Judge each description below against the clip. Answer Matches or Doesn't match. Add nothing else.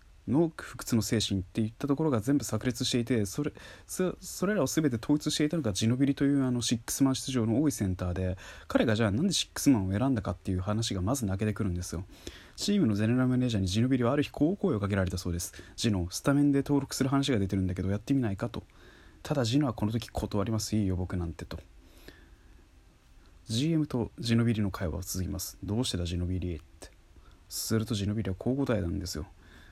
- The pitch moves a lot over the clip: Matches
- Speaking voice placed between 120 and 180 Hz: Doesn't match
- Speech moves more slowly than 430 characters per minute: Doesn't match